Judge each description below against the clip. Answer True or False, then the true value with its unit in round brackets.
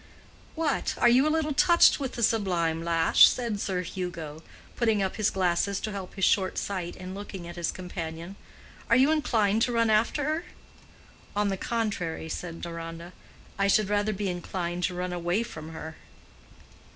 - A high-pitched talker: True (195 Hz)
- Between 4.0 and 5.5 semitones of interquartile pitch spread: True (4.5 semitones)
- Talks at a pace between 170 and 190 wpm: True (175 wpm)